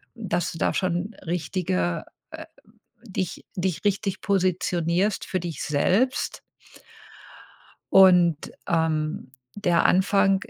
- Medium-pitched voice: Yes, medium, 180 Hz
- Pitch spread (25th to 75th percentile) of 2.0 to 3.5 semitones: Yes, average, 2.8 semitones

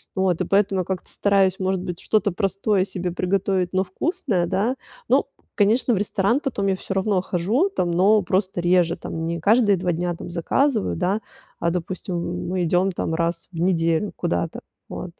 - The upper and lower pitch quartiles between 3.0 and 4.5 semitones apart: No, narrow, 2.5 semitones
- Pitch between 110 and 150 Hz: No, medium, 185 Hz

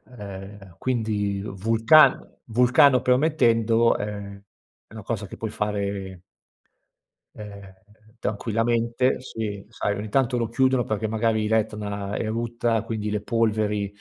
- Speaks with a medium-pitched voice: No, low, 110 Hz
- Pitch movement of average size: No, narrow, 2.3 semitones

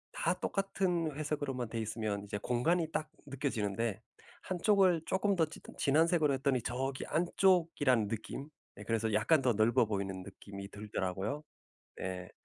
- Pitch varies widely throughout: Yes, wide, 7.0 semitones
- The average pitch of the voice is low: Yes, low, 130 Hz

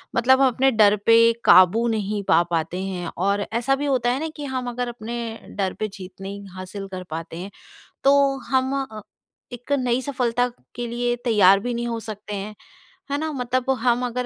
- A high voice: Yes, high, 235 Hz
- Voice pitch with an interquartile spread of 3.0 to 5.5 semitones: Yes, average, 3.9 semitones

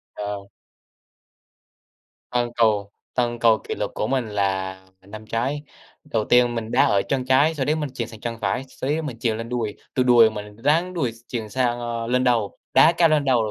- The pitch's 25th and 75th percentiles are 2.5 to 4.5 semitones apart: Yes, average, 3.0 semitones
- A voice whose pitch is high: No, low, 120 Hz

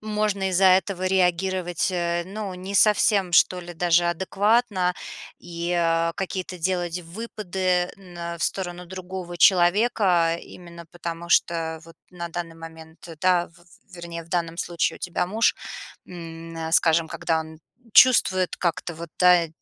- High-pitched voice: No, medium, 175 Hz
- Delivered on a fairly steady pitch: Yes, narrow, 1.8 semitones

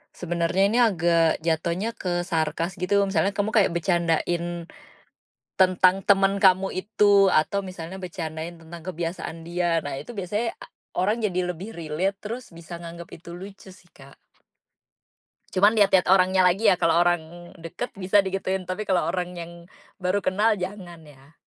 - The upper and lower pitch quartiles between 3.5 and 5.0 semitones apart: No, narrow, 2.5 semitones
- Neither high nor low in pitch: Yes, medium, 180 Hz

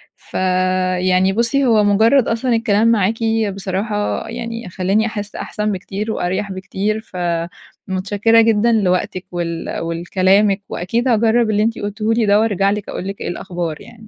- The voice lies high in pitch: Yes, high, 205 Hz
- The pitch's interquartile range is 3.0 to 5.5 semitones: Yes, average, 3.3 semitones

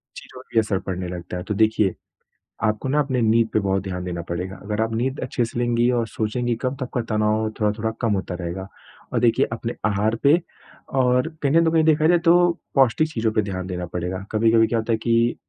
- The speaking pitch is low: Yes, low, 110 Hz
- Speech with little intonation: No, average, 4.1 semitones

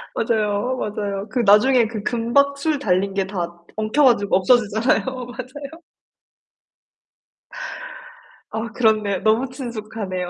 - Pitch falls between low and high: No, high, 220 Hz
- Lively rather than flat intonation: No, average, 3.9 semitones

